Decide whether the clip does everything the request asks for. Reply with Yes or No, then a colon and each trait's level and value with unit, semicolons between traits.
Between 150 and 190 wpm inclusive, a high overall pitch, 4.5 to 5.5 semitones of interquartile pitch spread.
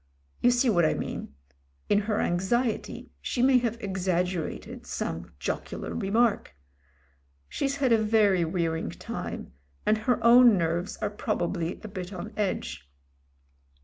No: average, 140 wpm; high, 200 Hz; average, 5.1 semitones